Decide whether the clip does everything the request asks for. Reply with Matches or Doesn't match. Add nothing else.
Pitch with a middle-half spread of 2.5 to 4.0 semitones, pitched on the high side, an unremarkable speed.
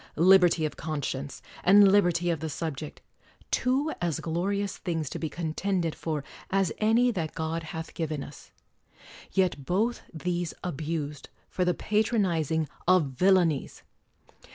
Doesn't match